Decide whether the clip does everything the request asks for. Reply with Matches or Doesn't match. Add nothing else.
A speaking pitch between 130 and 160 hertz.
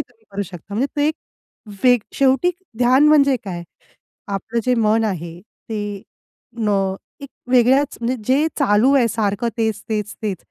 Doesn't match